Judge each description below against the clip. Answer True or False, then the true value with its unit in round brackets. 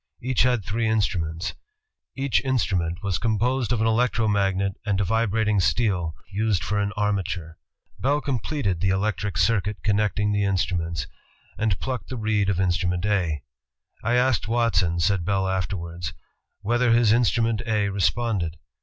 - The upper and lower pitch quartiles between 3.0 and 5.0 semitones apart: True (3.5 semitones)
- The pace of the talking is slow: False (155 wpm)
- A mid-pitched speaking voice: False (105 Hz)